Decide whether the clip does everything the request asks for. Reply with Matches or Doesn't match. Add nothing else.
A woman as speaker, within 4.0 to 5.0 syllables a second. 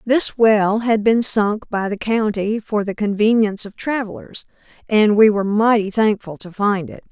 Matches